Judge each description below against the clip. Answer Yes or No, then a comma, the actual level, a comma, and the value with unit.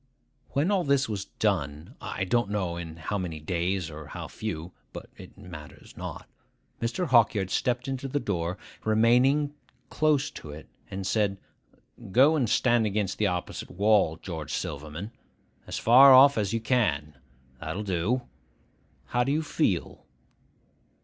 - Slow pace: No, average, 145 wpm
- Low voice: Yes, low, 105 Hz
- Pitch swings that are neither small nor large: No, wide, 6.4 semitones